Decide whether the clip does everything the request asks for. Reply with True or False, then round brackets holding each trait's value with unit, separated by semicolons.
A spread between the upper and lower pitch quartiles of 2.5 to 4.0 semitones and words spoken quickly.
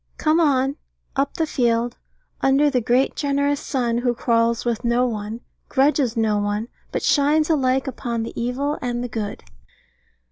False (3.2 semitones; 155 wpm)